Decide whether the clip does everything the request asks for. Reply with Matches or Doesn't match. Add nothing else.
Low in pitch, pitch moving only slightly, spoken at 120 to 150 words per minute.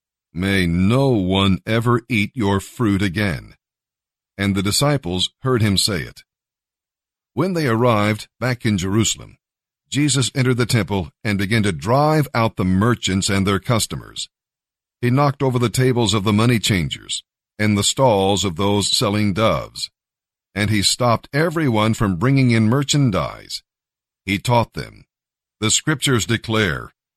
Doesn't match